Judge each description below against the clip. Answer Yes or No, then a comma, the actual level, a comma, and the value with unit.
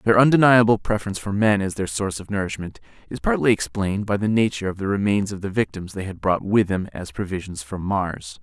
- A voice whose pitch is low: Yes, low, 100 Hz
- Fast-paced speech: Yes, fast, 220 wpm